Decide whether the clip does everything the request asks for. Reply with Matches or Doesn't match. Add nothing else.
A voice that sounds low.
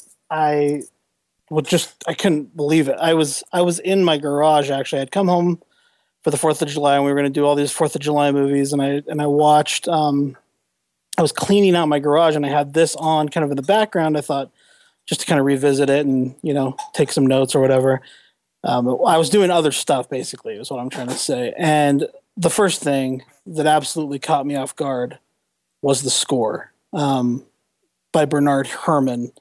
Doesn't match